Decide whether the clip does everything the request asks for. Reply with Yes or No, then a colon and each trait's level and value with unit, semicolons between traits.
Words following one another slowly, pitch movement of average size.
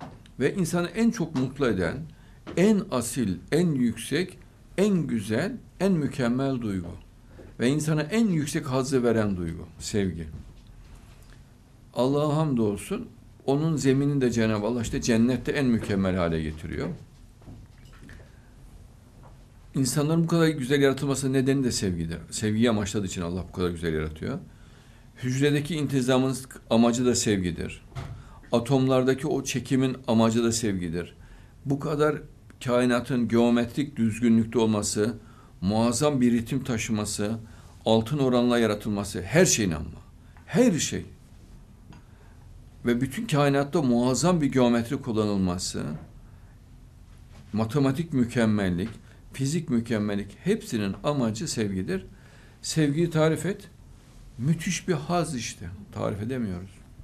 No: average, 110 wpm; average, 4.4 semitones